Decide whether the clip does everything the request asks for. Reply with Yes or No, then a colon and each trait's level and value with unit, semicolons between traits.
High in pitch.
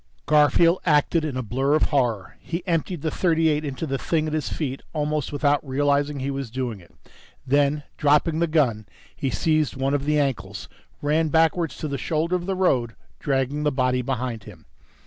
No: medium, 145 Hz